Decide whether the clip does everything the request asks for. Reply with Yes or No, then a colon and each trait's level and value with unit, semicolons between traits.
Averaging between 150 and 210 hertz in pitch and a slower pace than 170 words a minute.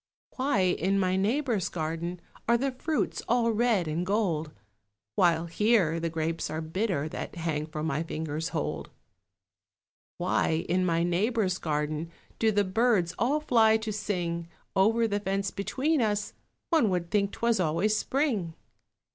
Yes: high, 190 Hz; average, 145 wpm